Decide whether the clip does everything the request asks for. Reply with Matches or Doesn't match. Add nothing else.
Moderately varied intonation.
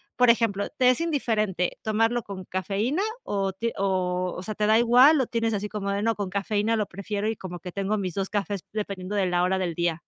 Matches